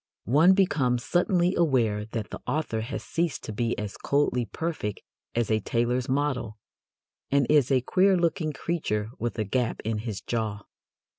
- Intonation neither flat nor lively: No, wide, 6.0 semitones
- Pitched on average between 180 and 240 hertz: No, low, 125 Hz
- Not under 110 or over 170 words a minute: Yes, average, 160 wpm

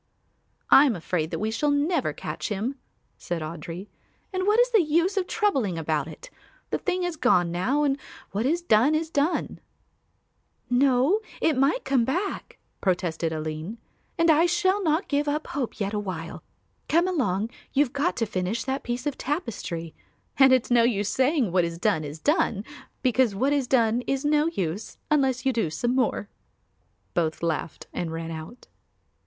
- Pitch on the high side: Yes, very high, 250 Hz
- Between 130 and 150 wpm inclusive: No, average, 175 wpm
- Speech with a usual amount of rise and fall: No, wide, 8.4 semitones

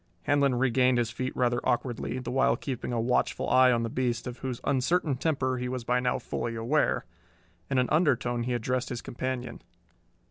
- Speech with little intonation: Yes, narrow, 1.2 semitones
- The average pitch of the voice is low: Yes, low, 125 Hz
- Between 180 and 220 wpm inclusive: Yes, average, 185 wpm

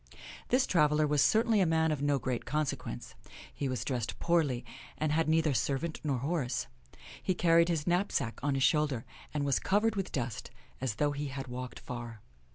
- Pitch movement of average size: Yes, average, 4.1 semitones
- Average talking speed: Yes, average, 180 wpm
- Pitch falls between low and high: Yes, medium, 145 Hz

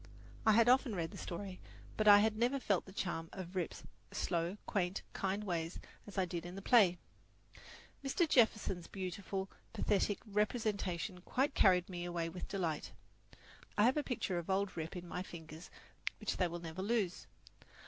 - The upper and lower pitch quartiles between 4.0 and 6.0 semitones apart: No, average, 3.3 semitones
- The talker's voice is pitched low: No, high, 190 Hz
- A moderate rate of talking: Yes, average, 170 wpm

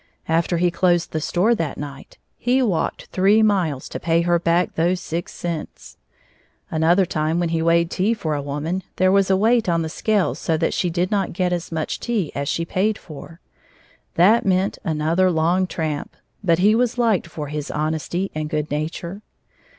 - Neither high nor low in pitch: Yes, medium, 170 Hz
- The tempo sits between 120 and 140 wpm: No, average, 190 wpm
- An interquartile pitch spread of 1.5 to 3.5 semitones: Yes, average, 3.0 semitones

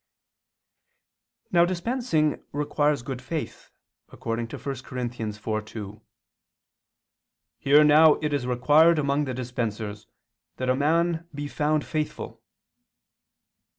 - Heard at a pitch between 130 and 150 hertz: Yes, medium, 140 Hz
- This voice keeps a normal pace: No, slow, 105 wpm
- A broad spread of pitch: No, average, 4.1 semitones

